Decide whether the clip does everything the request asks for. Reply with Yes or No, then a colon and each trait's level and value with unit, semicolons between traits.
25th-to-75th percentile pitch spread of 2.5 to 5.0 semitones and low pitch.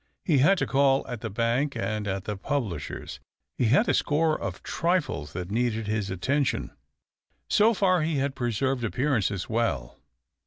No: wide, 5.5 semitones; low, 120 Hz